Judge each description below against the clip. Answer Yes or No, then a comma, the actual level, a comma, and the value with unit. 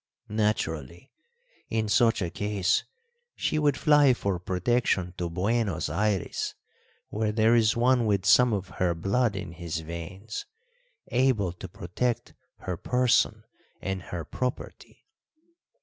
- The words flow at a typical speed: No, slow, 125 wpm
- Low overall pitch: Yes, low, 100 Hz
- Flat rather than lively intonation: No, average, 5.1 semitones